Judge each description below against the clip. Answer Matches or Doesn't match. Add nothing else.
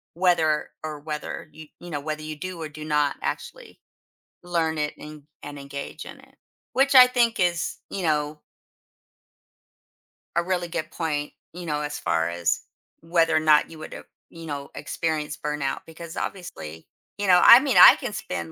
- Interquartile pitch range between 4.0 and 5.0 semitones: Doesn't match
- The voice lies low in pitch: Doesn't match